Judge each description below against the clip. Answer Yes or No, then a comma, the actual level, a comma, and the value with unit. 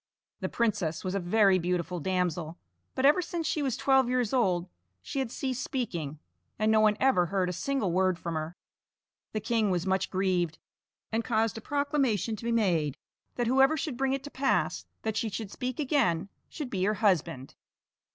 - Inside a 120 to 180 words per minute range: No, average, 190 wpm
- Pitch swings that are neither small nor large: No, wide, 6.3 semitones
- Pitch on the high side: Yes, high, 215 Hz